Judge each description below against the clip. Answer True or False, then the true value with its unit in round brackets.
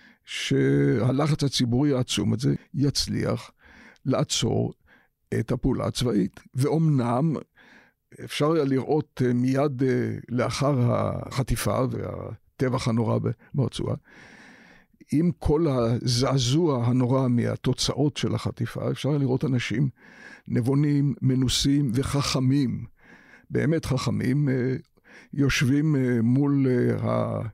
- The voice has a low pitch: True (130 Hz)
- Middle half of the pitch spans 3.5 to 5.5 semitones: False (2.7 semitones)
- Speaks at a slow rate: True (85 wpm)